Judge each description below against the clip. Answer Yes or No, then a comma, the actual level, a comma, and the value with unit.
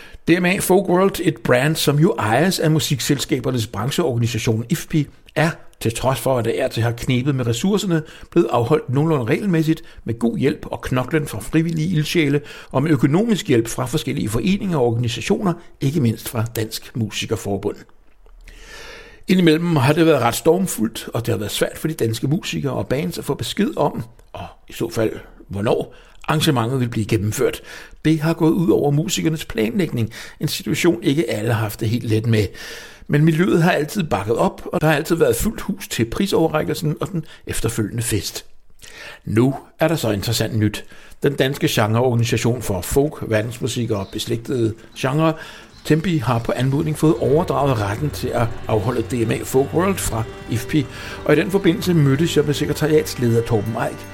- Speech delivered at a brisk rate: No, average, 175 wpm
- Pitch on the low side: No, medium, 145 Hz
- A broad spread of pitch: Yes, wide, 5.8 semitones